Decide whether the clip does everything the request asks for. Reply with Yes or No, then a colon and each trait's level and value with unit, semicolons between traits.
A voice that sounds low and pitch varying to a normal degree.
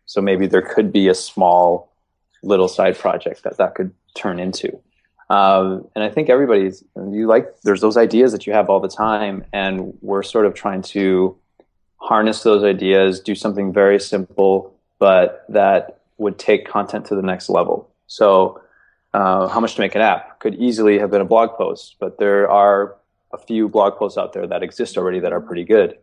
No: low, 100 Hz; narrow, 1.9 semitones